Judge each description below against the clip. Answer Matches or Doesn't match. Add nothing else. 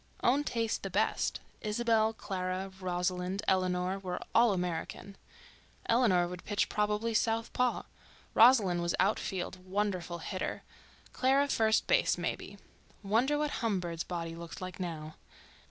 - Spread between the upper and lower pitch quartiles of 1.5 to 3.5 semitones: Doesn't match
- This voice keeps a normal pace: Doesn't match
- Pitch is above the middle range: Matches